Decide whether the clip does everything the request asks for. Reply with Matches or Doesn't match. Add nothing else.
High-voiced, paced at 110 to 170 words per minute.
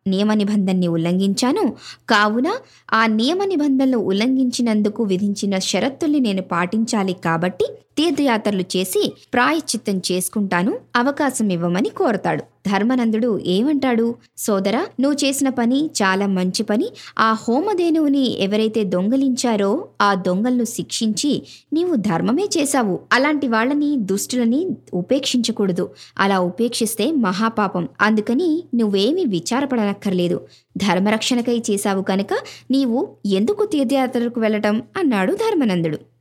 Doesn't match